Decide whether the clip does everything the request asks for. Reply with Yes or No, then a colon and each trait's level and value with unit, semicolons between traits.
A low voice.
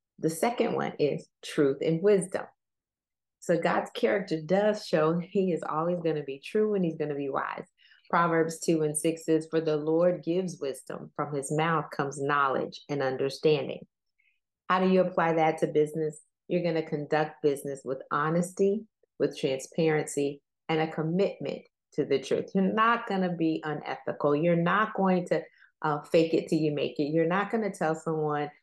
No: medium, 160 Hz